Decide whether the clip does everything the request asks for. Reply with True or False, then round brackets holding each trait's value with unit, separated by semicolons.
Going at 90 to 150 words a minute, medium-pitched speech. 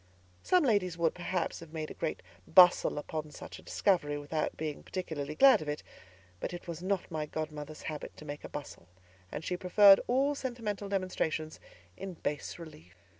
False (175 wpm; 165 Hz)